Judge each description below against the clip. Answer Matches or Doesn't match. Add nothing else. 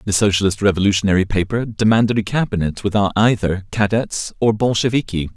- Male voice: Matches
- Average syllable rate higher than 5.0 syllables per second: Matches